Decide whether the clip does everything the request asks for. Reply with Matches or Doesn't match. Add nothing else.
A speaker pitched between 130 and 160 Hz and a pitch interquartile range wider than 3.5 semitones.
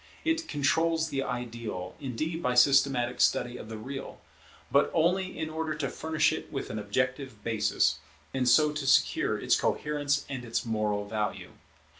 Matches